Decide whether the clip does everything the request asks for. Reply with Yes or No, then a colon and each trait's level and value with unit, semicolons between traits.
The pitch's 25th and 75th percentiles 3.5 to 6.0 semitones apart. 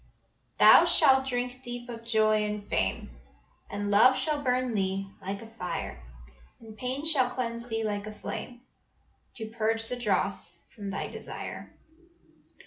No: average, 3.1 semitones